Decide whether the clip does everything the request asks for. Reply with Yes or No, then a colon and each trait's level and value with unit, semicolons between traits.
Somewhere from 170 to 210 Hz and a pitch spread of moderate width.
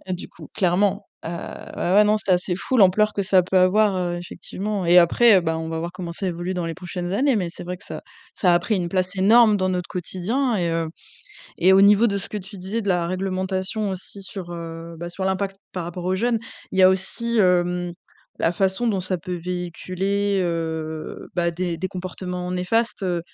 No: medium, 185 Hz; narrow, 2.3 semitones